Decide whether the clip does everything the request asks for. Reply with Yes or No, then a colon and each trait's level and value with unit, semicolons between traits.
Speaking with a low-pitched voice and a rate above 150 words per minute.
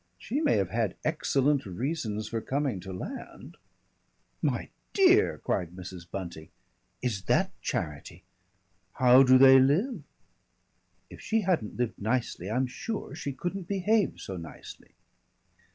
No: low, 130 Hz; slow, 135 wpm